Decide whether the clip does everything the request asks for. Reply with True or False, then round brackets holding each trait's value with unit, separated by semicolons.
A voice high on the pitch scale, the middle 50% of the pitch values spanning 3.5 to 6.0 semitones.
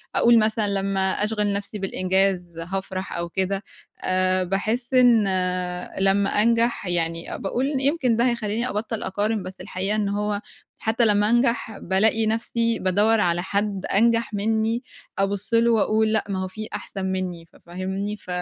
False (205 Hz; 2.9 semitones)